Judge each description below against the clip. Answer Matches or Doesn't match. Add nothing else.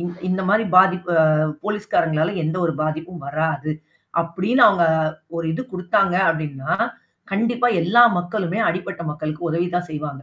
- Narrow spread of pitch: Doesn't match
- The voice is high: Doesn't match